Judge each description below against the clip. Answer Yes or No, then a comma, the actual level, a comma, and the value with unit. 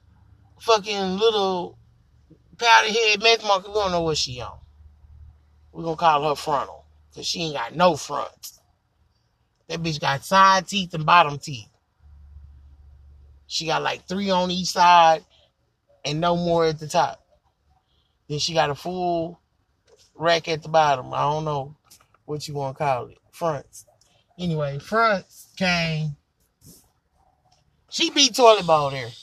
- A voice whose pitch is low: No, medium, 155 Hz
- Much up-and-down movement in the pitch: Yes, wide, 8.5 semitones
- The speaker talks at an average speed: Yes, average, 150 wpm